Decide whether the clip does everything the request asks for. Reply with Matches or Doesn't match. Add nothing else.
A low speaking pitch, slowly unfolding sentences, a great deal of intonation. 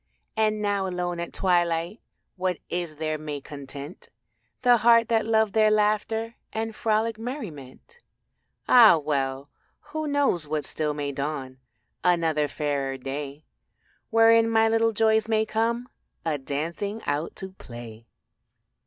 Doesn't match